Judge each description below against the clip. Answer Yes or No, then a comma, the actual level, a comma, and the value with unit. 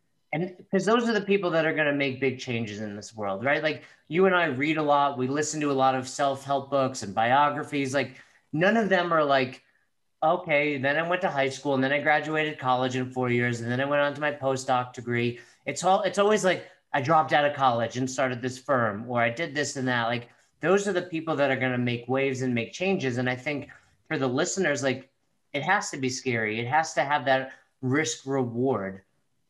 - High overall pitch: No, medium, 140 Hz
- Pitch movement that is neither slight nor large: Yes, average, 3.3 semitones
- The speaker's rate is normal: No, fast, 235 wpm